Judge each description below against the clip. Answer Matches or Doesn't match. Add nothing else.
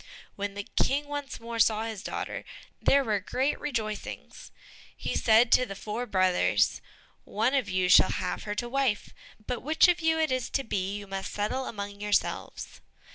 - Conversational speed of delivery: Matches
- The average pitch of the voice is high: Matches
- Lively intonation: Doesn't match